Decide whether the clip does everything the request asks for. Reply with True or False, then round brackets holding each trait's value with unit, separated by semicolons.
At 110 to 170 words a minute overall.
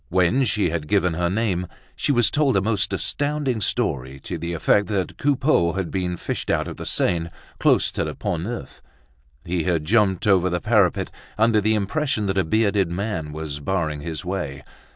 False (190 wpm)